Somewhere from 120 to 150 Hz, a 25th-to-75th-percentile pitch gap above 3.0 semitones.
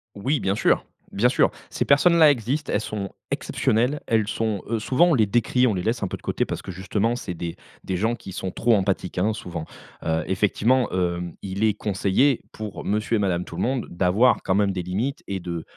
No: low, 105 Hz; average, 4.3 semitones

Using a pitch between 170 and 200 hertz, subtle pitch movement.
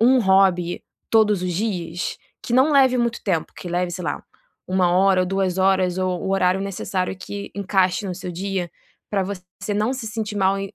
Yes: high, 190 Hz; narrow, 2.2 semitones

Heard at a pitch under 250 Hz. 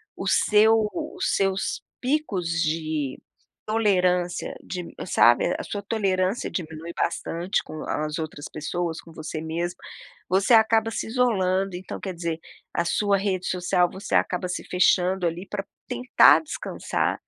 Yes: medium, 185 Hz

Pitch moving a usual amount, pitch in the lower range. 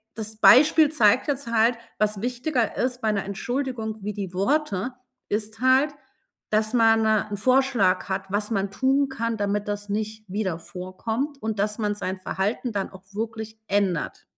No: average, 3.5 semitones; high, 220 Hz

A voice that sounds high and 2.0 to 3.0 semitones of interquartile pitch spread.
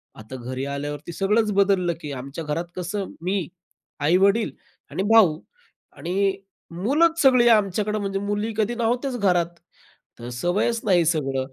No: high, 195 Hz; average, 5.1 semitones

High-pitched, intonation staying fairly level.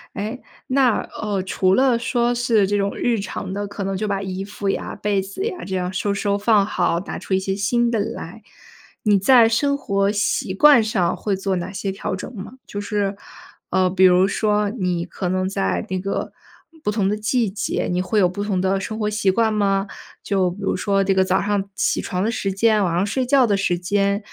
Yes: high, 200 Hz; narrow, 2.2 semitones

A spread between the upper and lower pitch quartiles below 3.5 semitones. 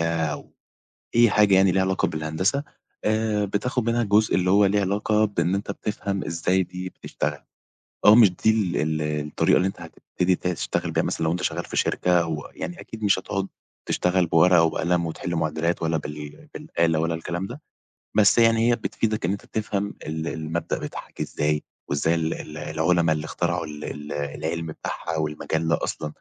No: average, 4.0 semitones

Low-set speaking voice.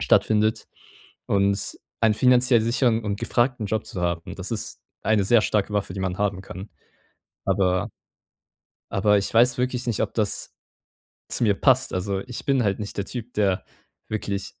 Yes: low, 105 Hz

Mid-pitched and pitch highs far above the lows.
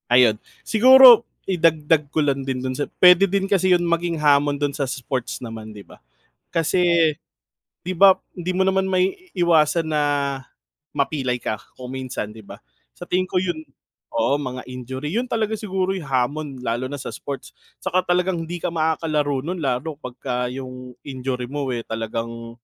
Yes: medium, 150 Hz; wide, 5.8 semitones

